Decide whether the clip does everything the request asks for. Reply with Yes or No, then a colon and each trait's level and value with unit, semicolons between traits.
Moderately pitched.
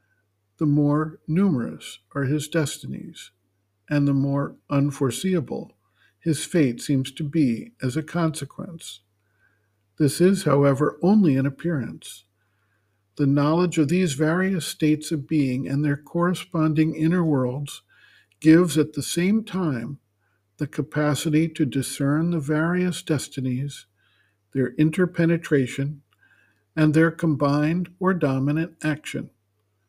Yes: medium, 150 Hz